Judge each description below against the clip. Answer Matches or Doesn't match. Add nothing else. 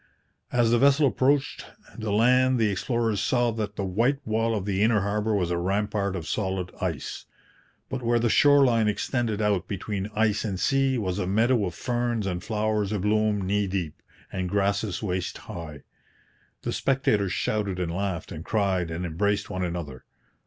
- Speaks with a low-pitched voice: Matches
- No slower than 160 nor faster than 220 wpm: Matches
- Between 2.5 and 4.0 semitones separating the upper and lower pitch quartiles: Matches